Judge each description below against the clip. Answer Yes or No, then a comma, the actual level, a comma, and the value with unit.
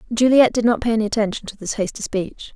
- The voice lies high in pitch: Yes, high, 220 Hz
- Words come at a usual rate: No, fast, 210 wpm